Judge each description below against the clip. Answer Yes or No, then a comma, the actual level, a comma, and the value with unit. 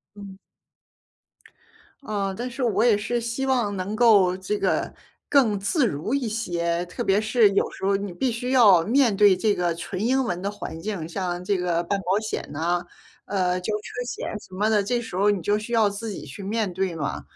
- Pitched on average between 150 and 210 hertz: Yes, high, 205 Hz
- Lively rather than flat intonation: No, average, 3.8 semitones